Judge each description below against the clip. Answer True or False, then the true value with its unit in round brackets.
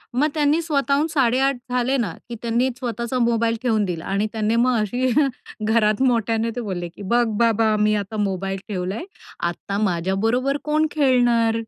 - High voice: True (230 Hz)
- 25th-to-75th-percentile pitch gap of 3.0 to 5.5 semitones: True (3.5 semitones)